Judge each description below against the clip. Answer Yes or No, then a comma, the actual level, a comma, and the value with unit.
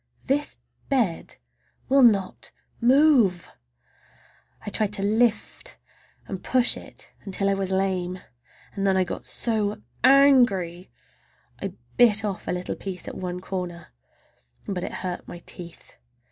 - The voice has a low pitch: No, high, 195 Hz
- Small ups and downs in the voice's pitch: No, average, 4.5 semitones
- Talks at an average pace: No, slow, 130 wpm